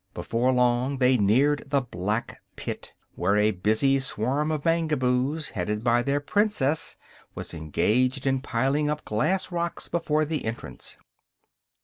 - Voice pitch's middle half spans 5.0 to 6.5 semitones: No, average, 4.5 semitones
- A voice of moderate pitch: No, low, 130 Hz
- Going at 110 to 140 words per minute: Yes, slow, 135 wpm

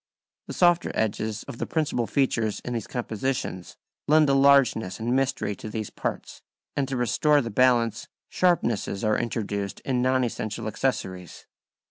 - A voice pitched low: Yes, low, 120 Hz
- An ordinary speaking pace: Yes, average, 150 wpm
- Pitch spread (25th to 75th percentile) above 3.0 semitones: Yes, average, 3.8 semitones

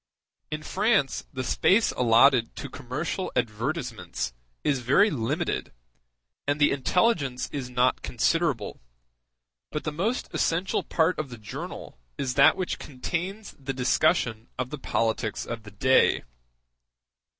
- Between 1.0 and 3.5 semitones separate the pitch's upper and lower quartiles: No, average, 5.3 semitones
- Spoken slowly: Yes, slow, 130 wpm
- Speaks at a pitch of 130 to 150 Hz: Yes, low, 135 Hz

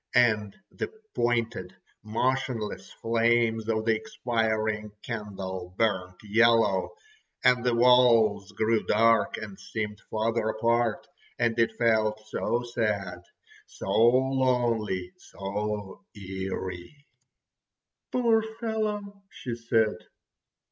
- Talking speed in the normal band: No, slow, 90 wpm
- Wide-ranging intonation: No, narrow, 2.5 semitones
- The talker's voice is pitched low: Yes, low, 115 Hz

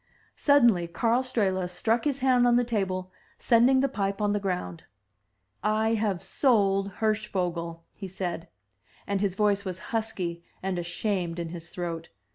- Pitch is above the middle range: Yes, high, 195 Hz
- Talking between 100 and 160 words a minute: Yes, average, 150 wpm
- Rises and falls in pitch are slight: No, average, 4.1 semitones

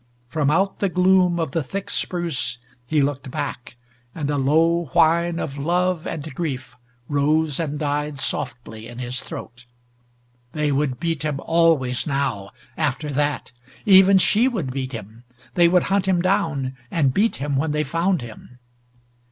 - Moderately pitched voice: Yes, medium, 150 Hz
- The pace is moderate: Yes, average, 160 wpm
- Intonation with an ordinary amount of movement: Yes, average, 4.2 semitones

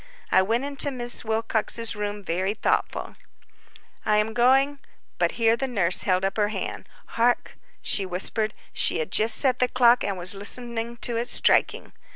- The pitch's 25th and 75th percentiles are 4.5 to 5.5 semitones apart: No, average, 3.0 semitones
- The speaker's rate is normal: Yes, average, 170 wpm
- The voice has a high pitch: Yes, high, 225 Hz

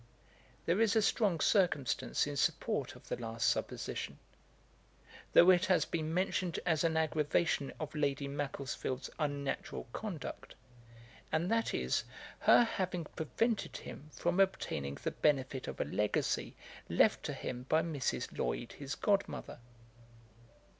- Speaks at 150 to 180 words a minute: No, slow, 135 wpm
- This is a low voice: No, medium, 155 Hz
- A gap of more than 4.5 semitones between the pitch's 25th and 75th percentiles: Yes, average, 4.9 semitones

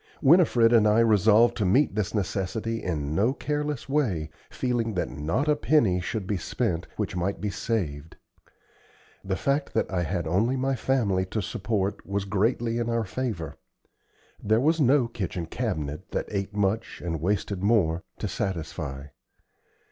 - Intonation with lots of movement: No, average, 4.7 semitones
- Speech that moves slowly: No, average, 155 wpm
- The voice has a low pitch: Yes, low, 105 Hz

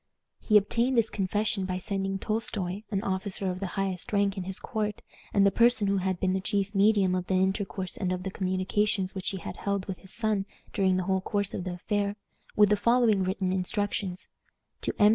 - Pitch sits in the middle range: No, high, 195 Hz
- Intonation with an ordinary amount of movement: No, narrow, 1.8 semitones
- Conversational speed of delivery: No, fast, 210 wpm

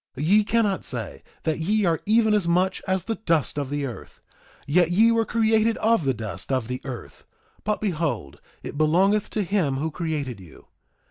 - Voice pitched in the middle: Yes, medium, 170 Hz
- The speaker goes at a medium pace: Yes, average, 185 wpm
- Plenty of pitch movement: Yes, wide, 7.0 semitones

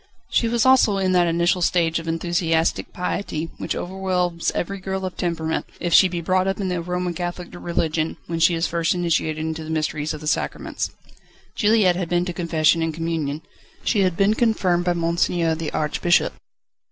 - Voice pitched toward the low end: No, medium, 175 Hz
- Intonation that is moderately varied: No, narrow, 2.0 semitones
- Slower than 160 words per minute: No, average, 185 wpm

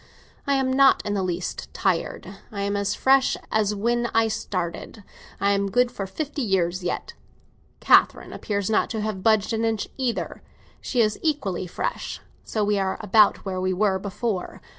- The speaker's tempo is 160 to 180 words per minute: Yes, average, 175 wpm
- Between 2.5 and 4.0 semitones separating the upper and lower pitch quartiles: Yes, average, 3.1 semitones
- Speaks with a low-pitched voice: No, high, 205 Hz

